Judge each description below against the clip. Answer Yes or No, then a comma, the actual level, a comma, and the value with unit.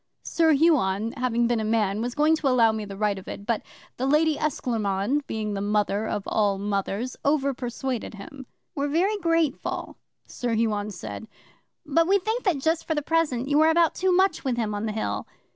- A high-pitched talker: Yes, high, 245 Hz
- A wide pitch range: Yes, wide, 6.5 semitones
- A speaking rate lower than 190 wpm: No, average, 200 wpm